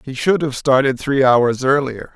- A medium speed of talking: Yes, average, 195 wpm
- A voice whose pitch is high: No, low, 135 Hz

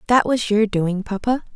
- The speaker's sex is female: Yes, female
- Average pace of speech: Yes, average, 195 wpm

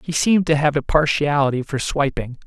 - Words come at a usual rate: Yes, average, 195 wpm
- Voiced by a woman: No, male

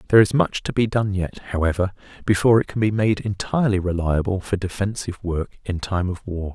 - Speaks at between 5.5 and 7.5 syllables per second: Yes, 5.9 syllables/s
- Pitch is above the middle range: No, low, 100 Hz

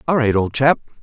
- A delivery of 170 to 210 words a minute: No, fast, 235 wpm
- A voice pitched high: No, low, 130 Hz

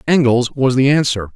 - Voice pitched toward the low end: Yes, low, 130 Hz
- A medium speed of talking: Yes, average, 175 wpm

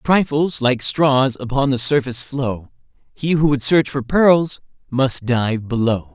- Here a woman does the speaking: No, male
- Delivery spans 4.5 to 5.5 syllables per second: No, 4.0 syllables/s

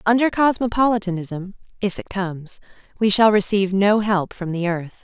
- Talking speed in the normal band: Yes, average, 155 wpm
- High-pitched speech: Yes, high, 200 Hz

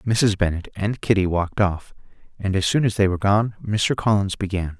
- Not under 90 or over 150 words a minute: No, average, 200 wpm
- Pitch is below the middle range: Yes, low, 100 Hz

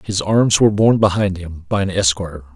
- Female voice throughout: No, male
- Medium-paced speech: No, fast, 210 wpm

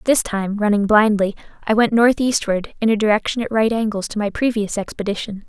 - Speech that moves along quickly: No, average, 185 wpm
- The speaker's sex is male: No, female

